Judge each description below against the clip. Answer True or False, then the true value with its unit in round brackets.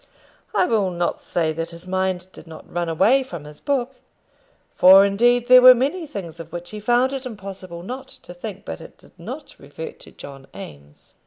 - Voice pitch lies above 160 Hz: True (190 Hz)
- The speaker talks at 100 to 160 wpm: False (195 wpm)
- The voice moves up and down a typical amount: False (6.5 semitones)